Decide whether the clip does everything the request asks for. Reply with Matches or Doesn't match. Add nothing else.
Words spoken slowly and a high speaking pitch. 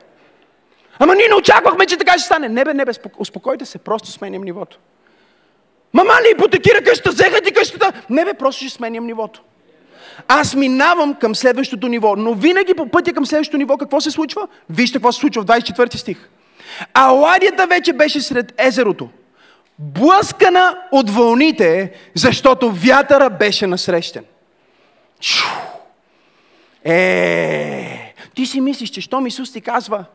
Doesn't match